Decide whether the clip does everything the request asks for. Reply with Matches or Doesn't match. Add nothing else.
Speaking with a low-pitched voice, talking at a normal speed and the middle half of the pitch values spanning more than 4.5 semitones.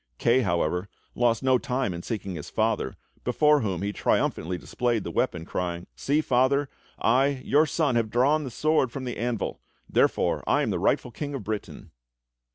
Matches